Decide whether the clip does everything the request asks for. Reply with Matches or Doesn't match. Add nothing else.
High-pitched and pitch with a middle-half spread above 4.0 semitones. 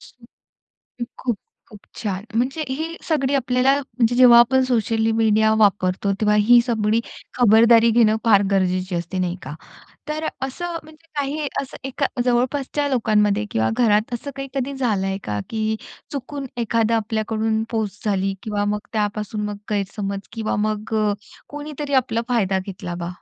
Doesn't match